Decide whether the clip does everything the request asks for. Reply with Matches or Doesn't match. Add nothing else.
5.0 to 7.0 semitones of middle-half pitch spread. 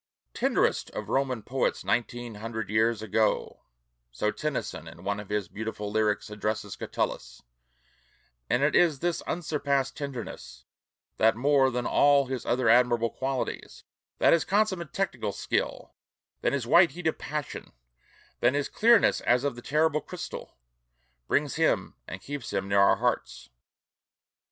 Matches